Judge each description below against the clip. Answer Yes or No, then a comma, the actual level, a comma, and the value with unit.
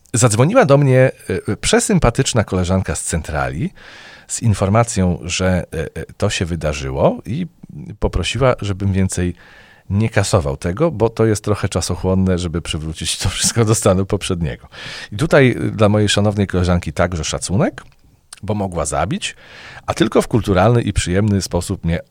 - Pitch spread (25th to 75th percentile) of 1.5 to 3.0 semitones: No, average, 4.1 semitones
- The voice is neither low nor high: No, low, 100 Hz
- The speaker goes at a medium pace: Yes, average, 140 wpm